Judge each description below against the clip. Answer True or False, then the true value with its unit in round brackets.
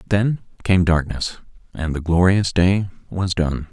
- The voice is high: False (90 Hz)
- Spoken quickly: False (145 wpm)